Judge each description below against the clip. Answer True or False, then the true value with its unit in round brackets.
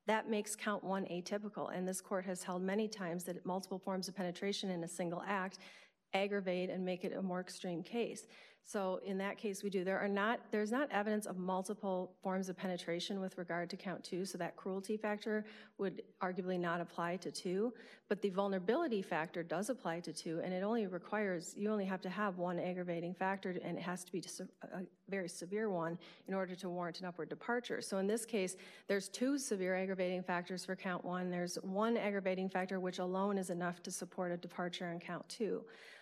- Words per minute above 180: True (205 wpm)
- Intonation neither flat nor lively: False (2.1 semitones)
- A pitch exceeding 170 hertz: True (185 Hz)